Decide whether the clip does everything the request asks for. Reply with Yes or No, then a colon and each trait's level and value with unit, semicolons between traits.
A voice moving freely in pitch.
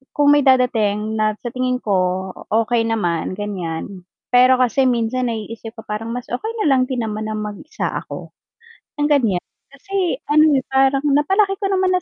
No: average, 4.6 semitones